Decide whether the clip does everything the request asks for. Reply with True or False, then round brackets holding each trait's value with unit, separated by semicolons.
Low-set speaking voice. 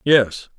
True (125 Hz)